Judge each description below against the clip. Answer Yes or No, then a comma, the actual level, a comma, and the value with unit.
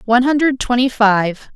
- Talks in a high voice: Yes, high, 240 Hz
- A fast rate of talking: No, average, 155 wpm